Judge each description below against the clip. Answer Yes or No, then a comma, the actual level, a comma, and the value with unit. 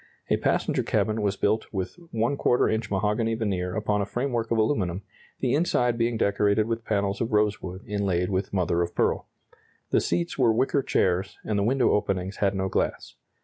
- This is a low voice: Yes, low, 105 Hz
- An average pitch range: Yes, average, 3.0 semitones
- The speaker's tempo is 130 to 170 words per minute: No, average, 180 wpm